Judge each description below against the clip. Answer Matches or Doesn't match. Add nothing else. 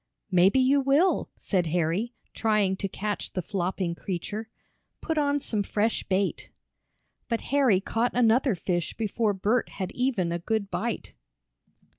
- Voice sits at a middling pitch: Doesn't match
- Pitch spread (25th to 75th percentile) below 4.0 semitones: Doesn't match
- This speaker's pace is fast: Doesn't match